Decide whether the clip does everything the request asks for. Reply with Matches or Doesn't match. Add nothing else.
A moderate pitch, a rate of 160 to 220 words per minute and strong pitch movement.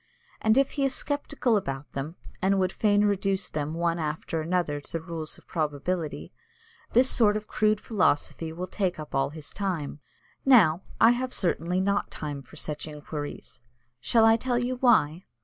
Matches